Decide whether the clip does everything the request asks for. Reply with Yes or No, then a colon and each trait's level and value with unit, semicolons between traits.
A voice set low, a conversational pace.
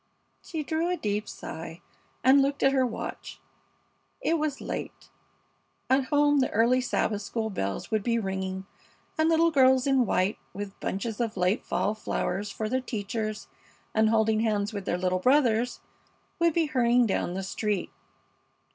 No: high, 225 Hz; average, 160 wpm